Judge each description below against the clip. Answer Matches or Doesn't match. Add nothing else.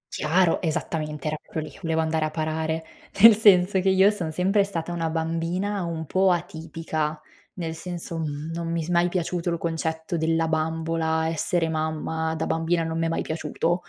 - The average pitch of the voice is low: Doesn't match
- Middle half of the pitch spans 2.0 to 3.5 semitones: Doesn't match